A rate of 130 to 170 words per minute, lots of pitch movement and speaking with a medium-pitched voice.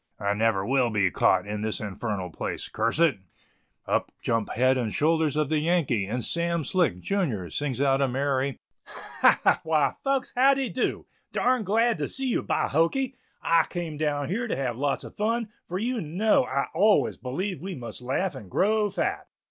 No: average, 190 wpm; wide, 8.0 semitones; medium, 150 Hz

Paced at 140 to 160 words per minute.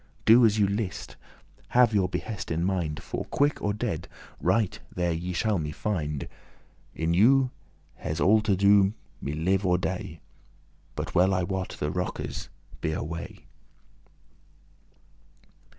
Yes: average, 150 wpm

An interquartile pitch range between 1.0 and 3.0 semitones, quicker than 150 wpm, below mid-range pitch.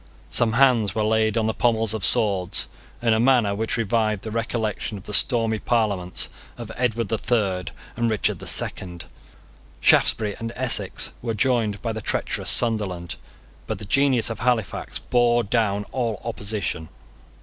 Yes: narrow, 2.4 semitones; average, 160 wpm; low, 110 Hz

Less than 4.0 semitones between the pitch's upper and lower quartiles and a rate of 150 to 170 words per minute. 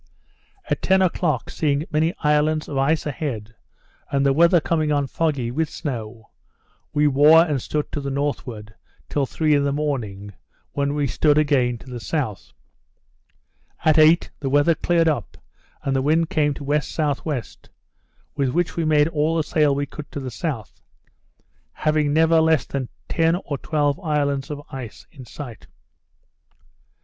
Yes: narrow, 2.5 semitones; average, 160 wpm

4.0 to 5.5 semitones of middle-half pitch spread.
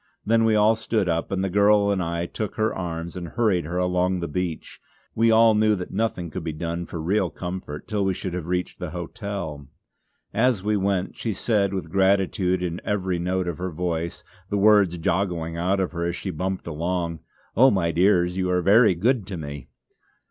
No: average, 2.9 semitones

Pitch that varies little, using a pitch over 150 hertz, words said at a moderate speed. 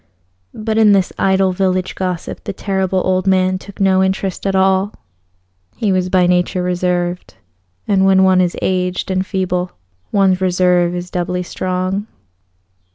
Yes: narrow, 1.0 semitones; medium, 185 Hz; average, 150 wpm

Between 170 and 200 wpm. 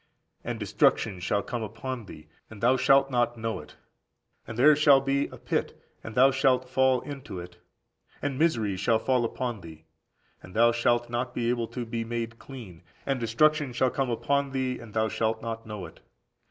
Yes: average, 190 wpm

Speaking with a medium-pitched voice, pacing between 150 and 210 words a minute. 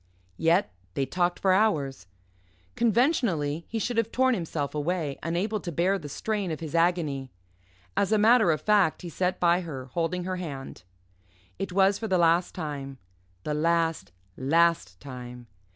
Yes: medium, 170 Hz; average, 160 wpm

